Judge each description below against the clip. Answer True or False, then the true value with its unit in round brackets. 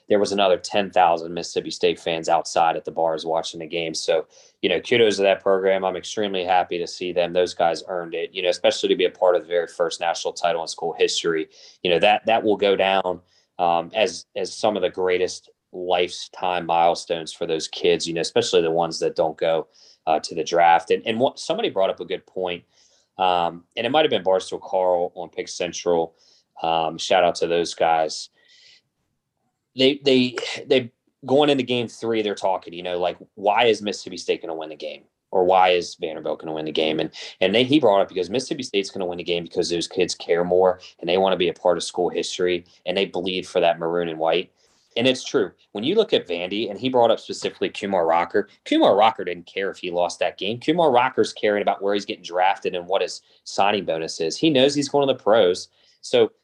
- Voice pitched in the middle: False (100 Hz)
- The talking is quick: True (230 wpm)